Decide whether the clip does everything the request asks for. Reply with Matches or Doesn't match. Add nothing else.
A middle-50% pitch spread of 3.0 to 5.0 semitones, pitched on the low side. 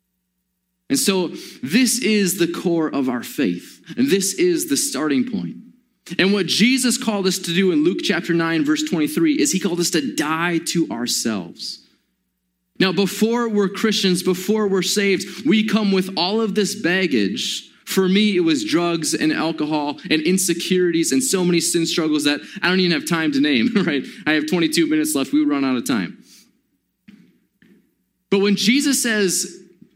Doesn't match